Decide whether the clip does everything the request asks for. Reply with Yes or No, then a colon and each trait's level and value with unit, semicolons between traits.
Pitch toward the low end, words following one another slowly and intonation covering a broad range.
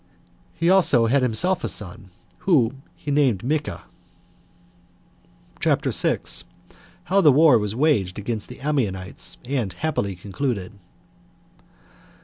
Yes: low, 125 Hz; slow, 115 wpm; wide, 6.3 semitones